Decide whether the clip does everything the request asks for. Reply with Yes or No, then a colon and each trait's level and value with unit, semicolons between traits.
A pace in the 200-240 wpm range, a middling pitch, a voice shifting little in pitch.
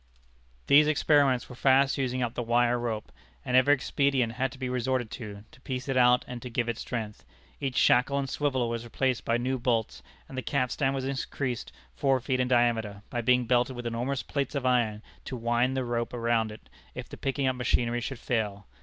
No: fast, 205 wpm; low, 125 Hz; narrow, 2.0 semitones